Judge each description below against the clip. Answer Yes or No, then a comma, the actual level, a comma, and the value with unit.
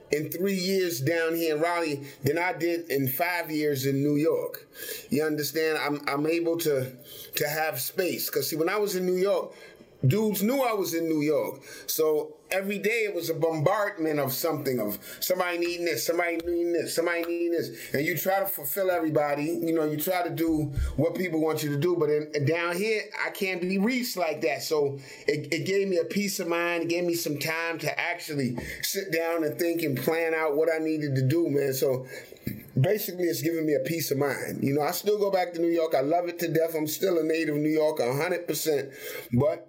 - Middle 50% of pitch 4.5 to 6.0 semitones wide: No, average, 3.2 semitones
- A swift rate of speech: Yes, fast, 220 wpm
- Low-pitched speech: No, medium, 165 Hz